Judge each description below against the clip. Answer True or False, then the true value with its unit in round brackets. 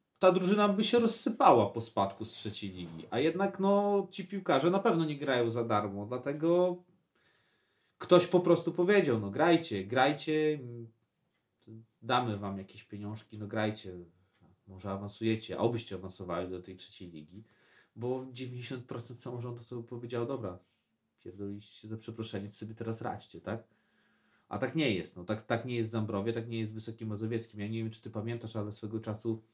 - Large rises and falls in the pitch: False (4.7 semitones)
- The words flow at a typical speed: False (175 wpm)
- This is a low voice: True (115 Hz)